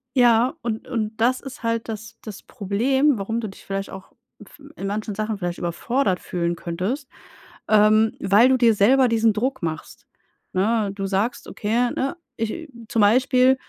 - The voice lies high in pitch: Yes, high, 220 Hz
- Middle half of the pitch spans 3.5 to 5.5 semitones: Yes, average, 3.8 semitones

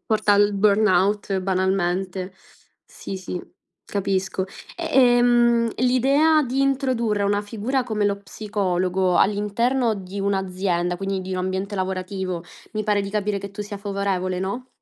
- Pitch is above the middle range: Yes, high, 200 Hz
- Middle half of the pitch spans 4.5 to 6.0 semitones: No, narrow, 2.6 semitones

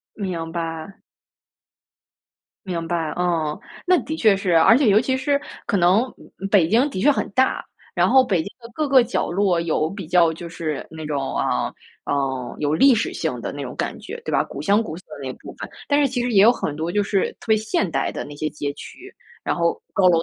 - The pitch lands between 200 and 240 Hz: No, medium, 185 Hz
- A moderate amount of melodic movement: No, wide, 5.9 semitones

